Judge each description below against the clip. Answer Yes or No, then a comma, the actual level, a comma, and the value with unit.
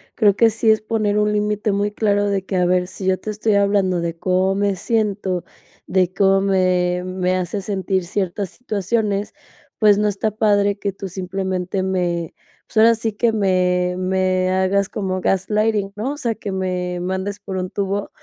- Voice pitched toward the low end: No, high, 195 Hz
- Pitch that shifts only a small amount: Yes, narrow, 2.1 semitones